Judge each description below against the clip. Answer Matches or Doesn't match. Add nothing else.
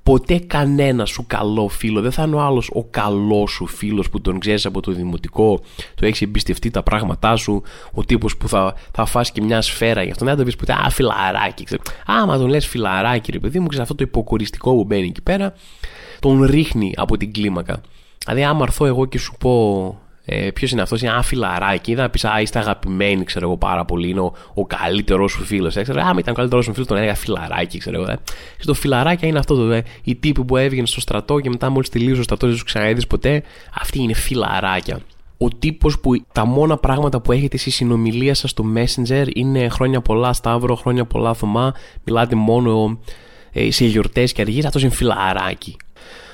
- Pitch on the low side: Matches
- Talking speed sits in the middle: Doesn't match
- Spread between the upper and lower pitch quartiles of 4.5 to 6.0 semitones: Doesn't match